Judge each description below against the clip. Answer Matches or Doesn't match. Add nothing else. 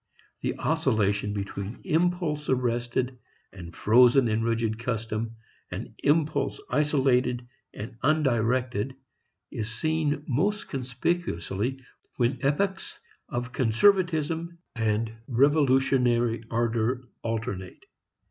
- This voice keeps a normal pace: Doesn't match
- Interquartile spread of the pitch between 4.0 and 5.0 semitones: Matches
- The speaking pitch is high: Doesn't match